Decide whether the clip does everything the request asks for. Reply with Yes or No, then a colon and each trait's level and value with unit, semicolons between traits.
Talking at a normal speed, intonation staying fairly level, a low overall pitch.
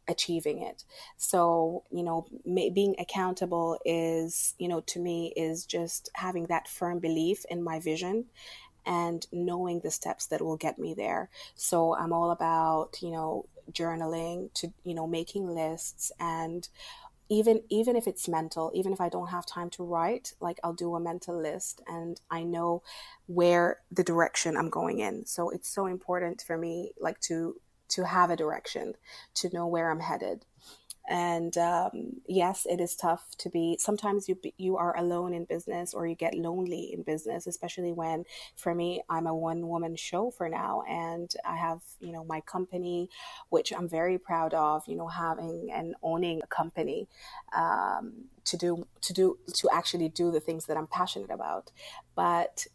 No: average, 175 wpm; narrow, 1.5 semitones; medium, 170 Hz